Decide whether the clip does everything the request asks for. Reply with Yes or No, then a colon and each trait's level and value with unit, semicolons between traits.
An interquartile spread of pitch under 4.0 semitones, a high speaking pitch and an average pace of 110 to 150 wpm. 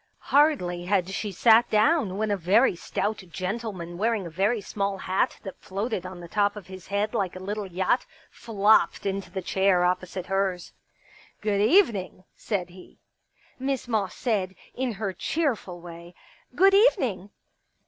No: average, 3.2 semitones; high, 200 Hz; average, 160 wpm